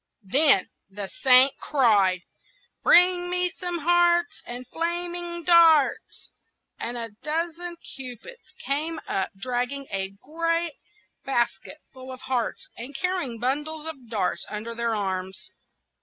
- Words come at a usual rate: No, slow, 120 wpm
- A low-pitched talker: No, very high, 275 Hz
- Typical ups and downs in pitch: No, wide, 6.3 semitones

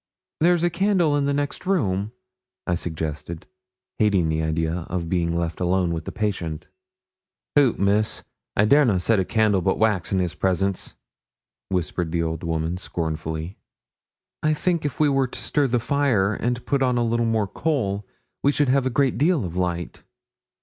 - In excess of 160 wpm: Yes, average, 175 wpm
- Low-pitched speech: Yes, low, 100 Hz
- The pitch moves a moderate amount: No, wide, 8.1 semitones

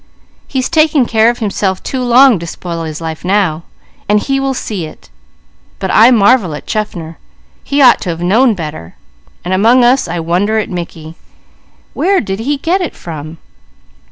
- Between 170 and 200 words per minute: Yes, average, 175 wpm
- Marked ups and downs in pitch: Yes, wide, 7.0 semitones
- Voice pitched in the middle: No, high, 205 Hz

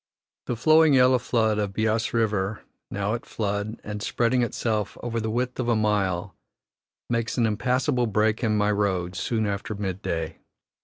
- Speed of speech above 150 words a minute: Yes, average, 165 wpm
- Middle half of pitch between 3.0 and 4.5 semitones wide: No, narrow, 2.6 semitones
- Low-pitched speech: Yes, low, 110 Hz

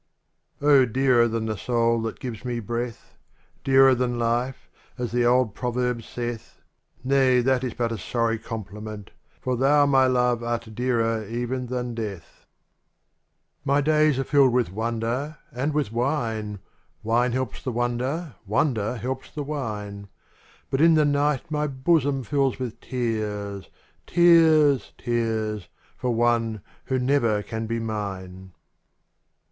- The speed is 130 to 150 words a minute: Yes, average, 145 wpm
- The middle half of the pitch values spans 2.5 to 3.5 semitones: Yes, average, 2.9 semitones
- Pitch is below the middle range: Yes, low, 120 Hz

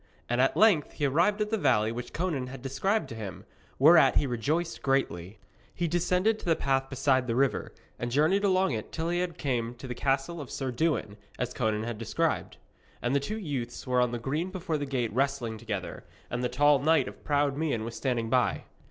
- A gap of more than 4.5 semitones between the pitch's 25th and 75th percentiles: Yes, average, 5.1 semitones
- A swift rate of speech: Yes, fast, 210 wpm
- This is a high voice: No, low, 135 Hz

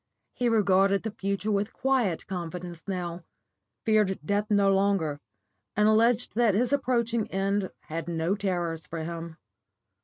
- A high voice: Yes, high, 195 Hz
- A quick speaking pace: No, average, 140 wpm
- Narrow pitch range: No, average, 3.8 semitones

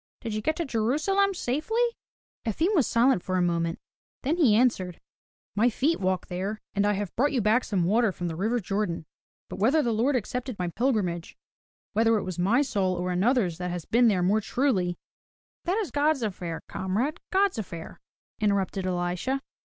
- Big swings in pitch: Yes, wide, 6.1 semitones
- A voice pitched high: Yes, high, 215 Hz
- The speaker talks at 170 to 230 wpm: Yes, average, 190 wpm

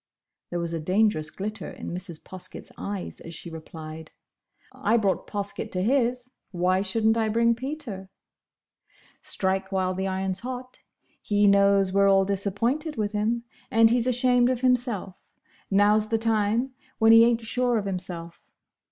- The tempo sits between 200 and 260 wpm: No, average, 155 wpm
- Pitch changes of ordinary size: Yes, average, 3.7 semitones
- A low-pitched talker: No, high, 205 Hz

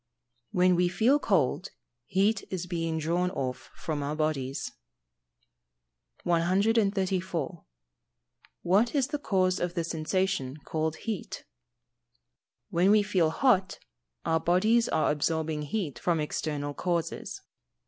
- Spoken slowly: Yes, slow, 115 wpm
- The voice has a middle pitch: Yes, medium, 175 Hz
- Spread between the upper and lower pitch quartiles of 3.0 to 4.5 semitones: Yes, average, 3.8 semitones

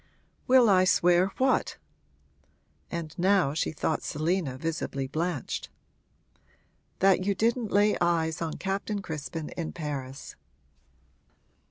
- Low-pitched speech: No, medium, 175 Hz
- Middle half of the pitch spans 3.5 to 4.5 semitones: Yes, average, 3.9 semitones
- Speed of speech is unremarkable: No, slow, 110 wpm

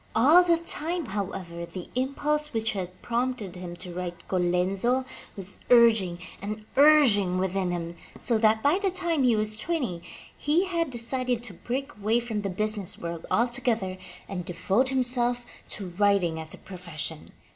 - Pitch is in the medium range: No, high, 215 Hz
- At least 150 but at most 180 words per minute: Yes, average, 155 wpm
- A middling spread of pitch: No, wide, 5.9 semitones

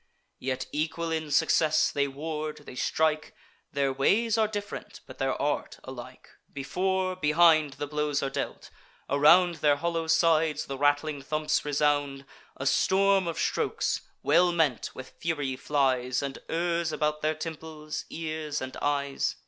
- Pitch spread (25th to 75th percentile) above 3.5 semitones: No, narrow, 2.6 semitones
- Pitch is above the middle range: No, medium, 150 Hz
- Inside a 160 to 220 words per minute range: No, average, 145 wpm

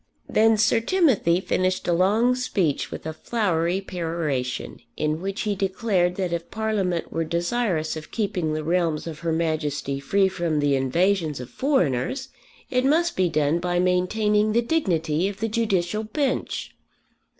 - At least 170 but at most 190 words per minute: No, average, 155 wpm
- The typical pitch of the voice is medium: Yes, medium, 180 Hz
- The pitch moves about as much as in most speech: Yes, average, 5.0 semitones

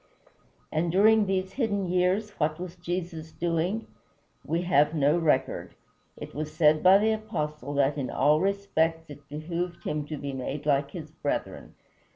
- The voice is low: No, medium, 165 Hz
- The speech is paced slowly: No, average, 160 wpm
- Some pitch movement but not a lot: Yes, average, 3.5 semitones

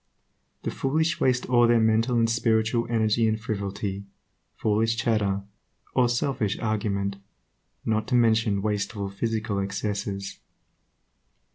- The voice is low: Yes, low, 110 Hz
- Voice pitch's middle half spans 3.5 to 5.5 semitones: No, narrow, 2.4 semitones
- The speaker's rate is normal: No, slow, 115 wpm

